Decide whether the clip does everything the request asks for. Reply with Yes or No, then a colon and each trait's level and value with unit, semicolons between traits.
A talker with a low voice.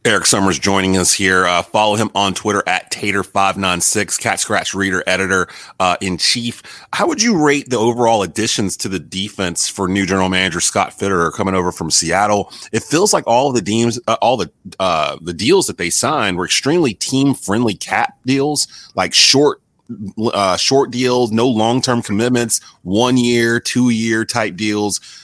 Yes: low, 105 Hz